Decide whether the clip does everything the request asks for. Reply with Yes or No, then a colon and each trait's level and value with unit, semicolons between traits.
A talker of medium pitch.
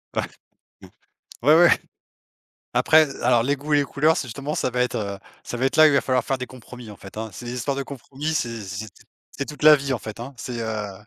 No: low, 130 Hz